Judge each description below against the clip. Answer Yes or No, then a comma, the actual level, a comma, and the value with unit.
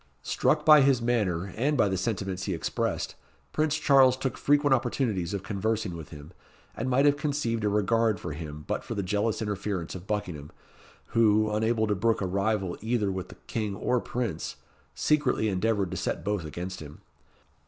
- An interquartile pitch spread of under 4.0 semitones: No, average, 4.3 semitones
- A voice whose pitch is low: Yes, low, 105 Hz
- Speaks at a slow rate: No, average, 180 wpm